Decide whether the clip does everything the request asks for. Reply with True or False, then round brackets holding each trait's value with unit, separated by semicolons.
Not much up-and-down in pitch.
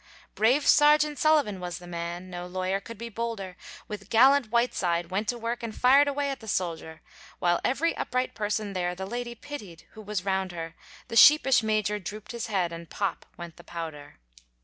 False (5.2 semitones)